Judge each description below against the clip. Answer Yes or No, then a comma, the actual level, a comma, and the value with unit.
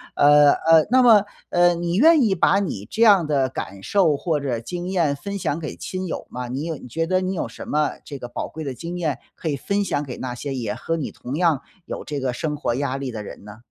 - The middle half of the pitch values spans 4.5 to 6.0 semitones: Yes, average, 4.9 semitones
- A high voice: No, medium, 155 Hz